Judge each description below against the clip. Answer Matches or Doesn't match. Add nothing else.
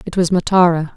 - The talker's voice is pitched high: Doesn't match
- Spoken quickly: Doesn't match